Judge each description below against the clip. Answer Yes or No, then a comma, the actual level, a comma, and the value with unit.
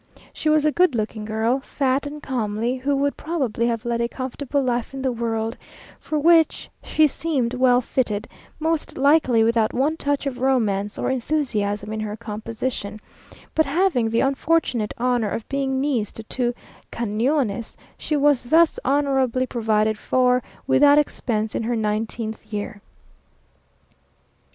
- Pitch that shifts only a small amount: No, average, 4.2 semitones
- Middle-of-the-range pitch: No, very high, 250 Hz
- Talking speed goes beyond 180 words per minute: No, average, 150 wpm